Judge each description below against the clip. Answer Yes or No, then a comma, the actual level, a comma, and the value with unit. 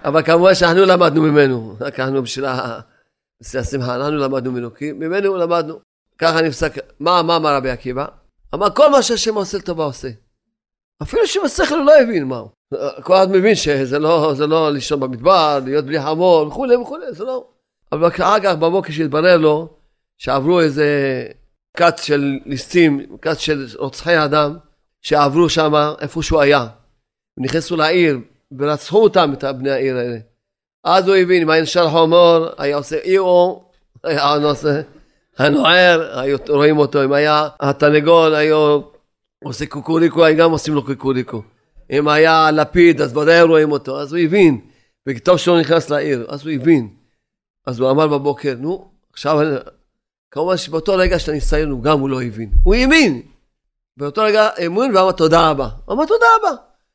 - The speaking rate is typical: No, fast, 160 wpm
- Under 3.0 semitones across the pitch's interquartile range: No, average, 3.6 semitones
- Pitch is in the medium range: Yes, medium, 155 Hz